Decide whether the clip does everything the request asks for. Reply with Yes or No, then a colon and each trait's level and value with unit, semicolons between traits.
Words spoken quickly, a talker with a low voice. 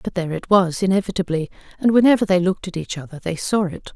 No: fast, 230 wpm; medium, 185 Hz